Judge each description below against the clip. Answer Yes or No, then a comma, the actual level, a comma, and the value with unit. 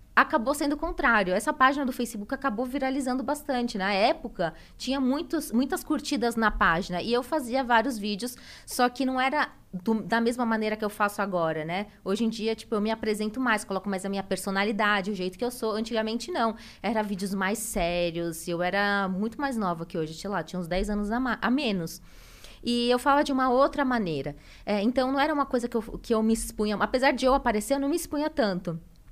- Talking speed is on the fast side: Yes, fast, 220 wpm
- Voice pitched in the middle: No, high, 225 Hz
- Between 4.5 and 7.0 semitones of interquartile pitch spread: Yes, average, 4.8 semitones